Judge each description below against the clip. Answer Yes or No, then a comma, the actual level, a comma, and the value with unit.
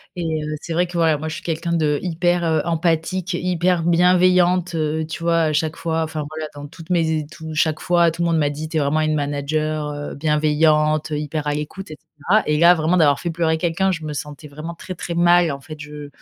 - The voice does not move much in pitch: Yes, narrow, 2.1 semitones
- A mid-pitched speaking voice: Yes, medium, 160 Hz